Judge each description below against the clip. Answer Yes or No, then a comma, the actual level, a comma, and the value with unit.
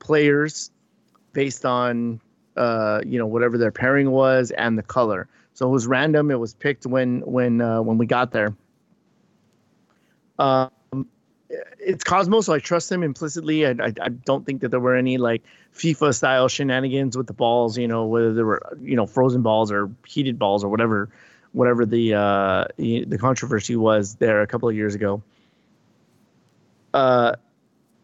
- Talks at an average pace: Yes, average, 170 wpm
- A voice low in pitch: Yes, low, 125 Hz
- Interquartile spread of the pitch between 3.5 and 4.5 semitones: No, average, 2.9 semitones